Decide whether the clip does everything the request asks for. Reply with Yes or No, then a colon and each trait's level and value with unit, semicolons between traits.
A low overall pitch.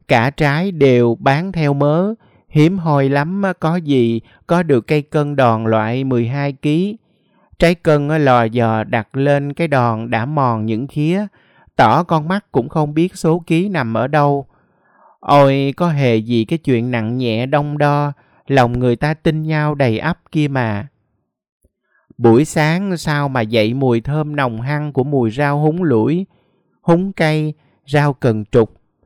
No: medium, 145 Hz